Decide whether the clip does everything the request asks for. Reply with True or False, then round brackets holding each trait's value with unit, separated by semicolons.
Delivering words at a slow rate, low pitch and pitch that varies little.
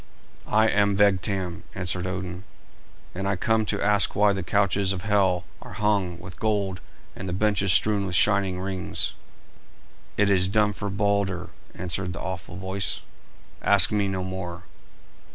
False (155 wpm; 95 Hz; 1.9 semitones)